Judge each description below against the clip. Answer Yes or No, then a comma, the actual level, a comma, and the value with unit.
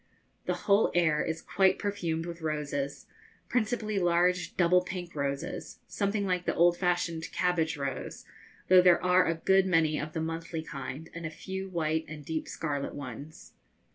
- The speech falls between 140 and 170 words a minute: Yes, average, 165 wpm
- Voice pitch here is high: No, medium, 170 Hz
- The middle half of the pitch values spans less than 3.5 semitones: Yes, average, 2.7 semitones